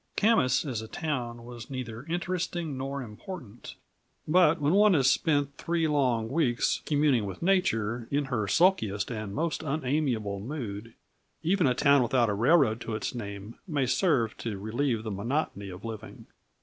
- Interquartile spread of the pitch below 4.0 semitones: No, wide, 5.6 semitones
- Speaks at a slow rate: No, average, 160 wpm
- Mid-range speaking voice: No, low, 130 Hz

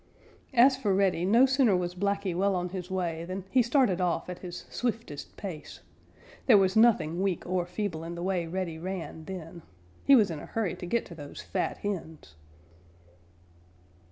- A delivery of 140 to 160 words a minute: No, average, 180 wpm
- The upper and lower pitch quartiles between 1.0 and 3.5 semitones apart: Yes, average, 2.9 semitones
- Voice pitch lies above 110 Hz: Yes, medium, 185 Hz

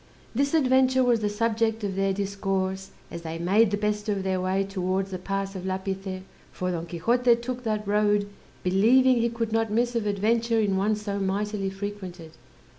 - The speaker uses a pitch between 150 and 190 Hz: No, high, 205 Hz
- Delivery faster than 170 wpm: Yes, average, 185 wpm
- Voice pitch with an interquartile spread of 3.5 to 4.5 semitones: No, average, 3.0 semitones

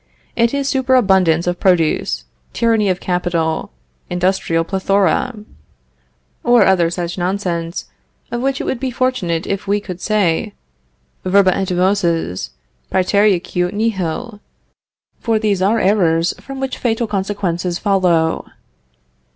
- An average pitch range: Yes, average, 3.6 semitones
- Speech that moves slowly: Yes, slow, 120 wpm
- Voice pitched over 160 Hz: Yes, high, 190 Hz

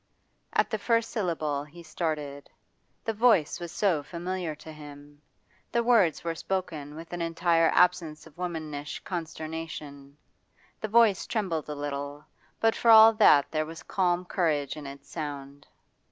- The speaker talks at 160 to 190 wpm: No, average, 150 wpm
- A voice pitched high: No, medium, 160 Hz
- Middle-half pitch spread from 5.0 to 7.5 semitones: No, average, 3.7 semitones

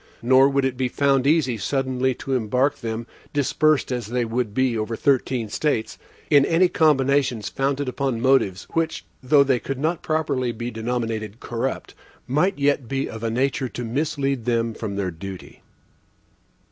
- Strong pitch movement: No, average, 3.2 semitones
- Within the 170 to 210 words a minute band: No, average, 160 wpm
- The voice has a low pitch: Yes, low, 130 Hz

